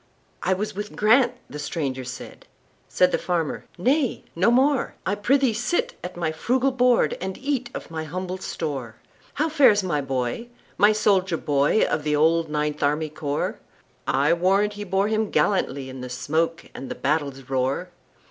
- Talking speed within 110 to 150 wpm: Yes, average, 140 wpm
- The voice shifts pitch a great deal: Yes, wide, 6.5 semitones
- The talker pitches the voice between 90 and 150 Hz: No, medium, 180 Hz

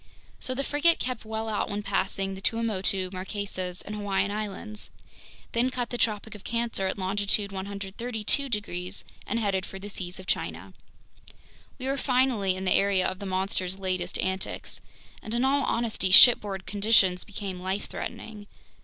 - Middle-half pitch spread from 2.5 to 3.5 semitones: Yes, average, 2.9 semitones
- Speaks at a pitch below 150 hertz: No, high, 200 Hz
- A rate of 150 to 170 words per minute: Yes, average, 160 wpm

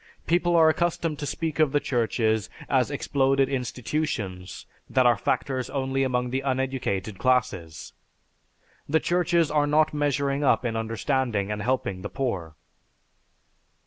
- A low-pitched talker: Yes, low, 130 Hz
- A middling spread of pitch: Yes, average, 4.6 semitones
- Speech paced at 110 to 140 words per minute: Yes, slow, 135 wpm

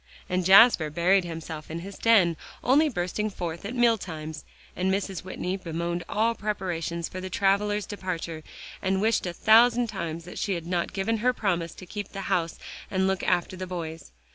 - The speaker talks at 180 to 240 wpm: Yes, average, 185 wpm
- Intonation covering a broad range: No, average, 3.4 semitones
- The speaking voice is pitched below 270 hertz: Yes, medium, 185 Hz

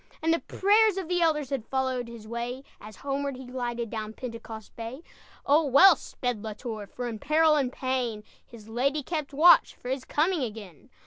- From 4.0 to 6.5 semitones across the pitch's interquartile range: Yes, average, 4.6 semitones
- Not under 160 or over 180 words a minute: No, average, 190 wpm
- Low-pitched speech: No, very high, 255 Hz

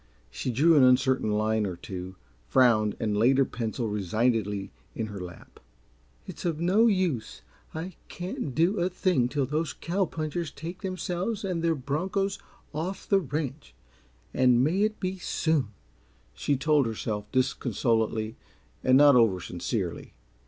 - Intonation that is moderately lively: No, wide, 7.6 semitones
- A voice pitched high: No, low, 135 Hz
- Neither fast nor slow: Yes, average, 145 wpm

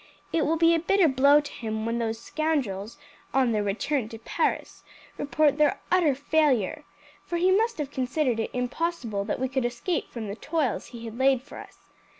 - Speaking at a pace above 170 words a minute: Yes, average, 190 wpm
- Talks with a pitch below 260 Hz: No, very high, 270 Hz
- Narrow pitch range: No, average, 5.2 semitones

